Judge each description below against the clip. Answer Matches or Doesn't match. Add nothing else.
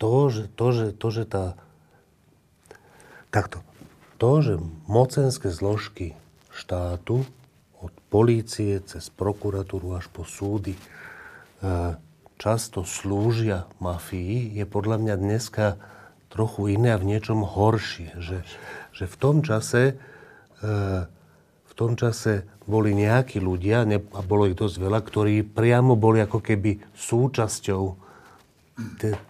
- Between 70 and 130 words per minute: Matches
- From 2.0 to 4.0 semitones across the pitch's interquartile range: Matches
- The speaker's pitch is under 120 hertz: Matches